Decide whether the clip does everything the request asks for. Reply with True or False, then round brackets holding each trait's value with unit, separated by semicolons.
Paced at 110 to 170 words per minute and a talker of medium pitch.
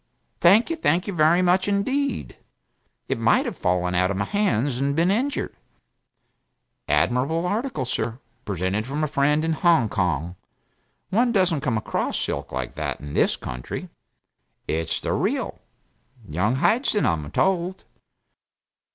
True (145 wpm; 150 Hz)